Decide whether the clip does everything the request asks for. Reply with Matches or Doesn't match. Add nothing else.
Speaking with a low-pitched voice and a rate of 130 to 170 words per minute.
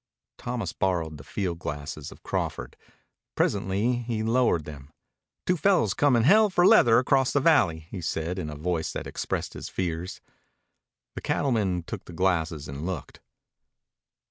Matches